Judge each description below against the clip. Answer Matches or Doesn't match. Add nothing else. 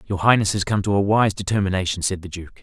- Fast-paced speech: Matches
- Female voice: Doesn't match